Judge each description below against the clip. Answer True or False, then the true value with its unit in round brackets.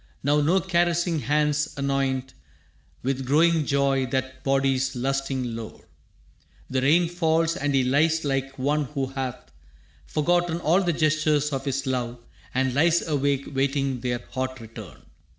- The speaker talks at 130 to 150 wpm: True (140 wpm)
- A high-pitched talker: False (140 Hz)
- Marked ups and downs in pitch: False (2.8 semitones)